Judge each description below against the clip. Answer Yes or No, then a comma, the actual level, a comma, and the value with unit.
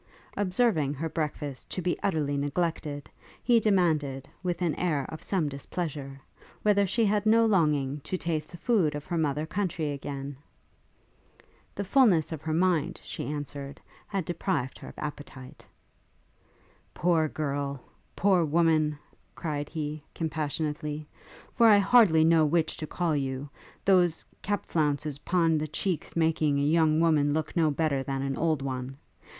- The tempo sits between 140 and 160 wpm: Yes, average, 150 wpm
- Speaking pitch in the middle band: Yes, medium, 155 Hz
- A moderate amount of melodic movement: Yes, average, 3.4 semitones